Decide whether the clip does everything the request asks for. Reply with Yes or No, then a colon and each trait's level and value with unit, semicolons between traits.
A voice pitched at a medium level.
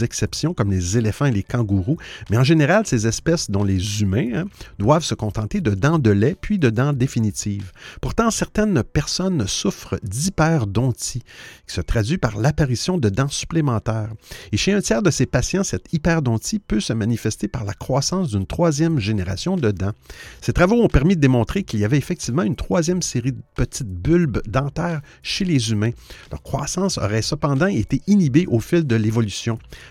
No: low, 125 Hz